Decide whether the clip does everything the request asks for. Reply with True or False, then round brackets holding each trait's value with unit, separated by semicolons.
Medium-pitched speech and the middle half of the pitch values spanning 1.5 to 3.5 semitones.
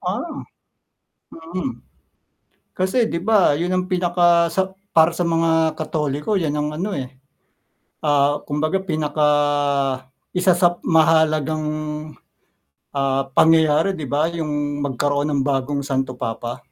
True (155 Hz; 3.2 semitones)